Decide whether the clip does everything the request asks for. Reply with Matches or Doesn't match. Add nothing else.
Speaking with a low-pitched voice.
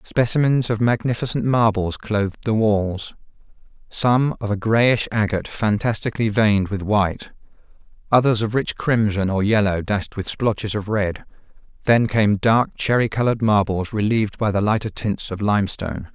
Matches